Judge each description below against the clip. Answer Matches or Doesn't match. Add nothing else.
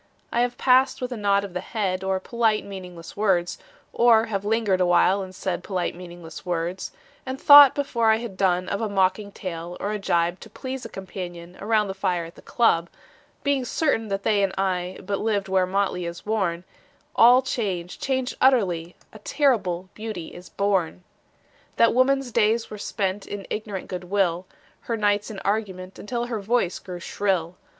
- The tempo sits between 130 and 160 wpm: Doesn't match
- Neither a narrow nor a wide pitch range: Matches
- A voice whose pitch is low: Doesn't match